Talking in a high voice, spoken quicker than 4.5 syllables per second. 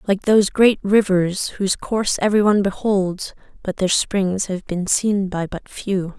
No: high, 195 Hz; 4.4 syllables/s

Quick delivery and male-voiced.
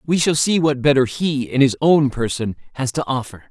Yes: fast, 225 wpm; male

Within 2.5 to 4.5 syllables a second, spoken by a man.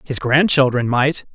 Yes: 4.2 syllables/s; male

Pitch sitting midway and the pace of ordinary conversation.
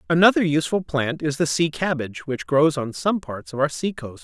No: medium, 150 Hz; fast, 225 wpm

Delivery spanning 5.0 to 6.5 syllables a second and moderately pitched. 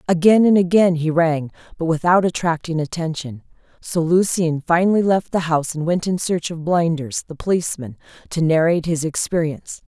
Yes: 5.4 syllables/s; medium, 165 Hz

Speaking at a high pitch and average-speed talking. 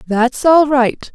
Yes: very high, 265 Hz; average, 155 wpm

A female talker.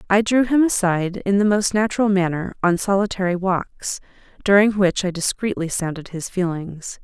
Yes: female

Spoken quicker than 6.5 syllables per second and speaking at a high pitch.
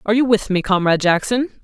Yes: 7.1 syllables/s; high, 210 Hz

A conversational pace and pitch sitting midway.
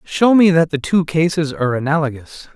Yes: average, 190 wpm; medium, 155 Hz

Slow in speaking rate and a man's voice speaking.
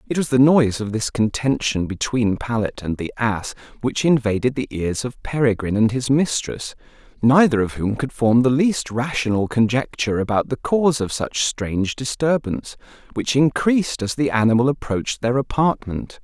No: average, 165 wpm; male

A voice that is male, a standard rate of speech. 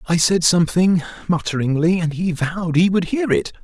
Yes: male; average, 180 wpm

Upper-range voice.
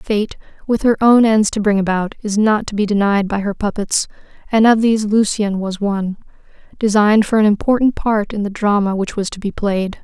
Yes: high, 210 Hz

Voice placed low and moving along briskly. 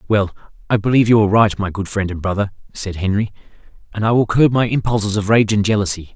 Yes: low, 105 Hz; fast, 225 wpm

